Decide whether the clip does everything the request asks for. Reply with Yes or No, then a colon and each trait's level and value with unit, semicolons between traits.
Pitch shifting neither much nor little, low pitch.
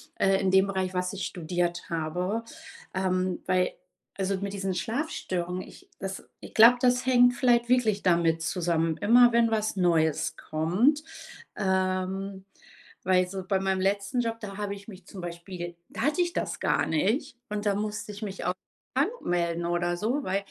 No: average, 3.2 semitones; high, 190 Hz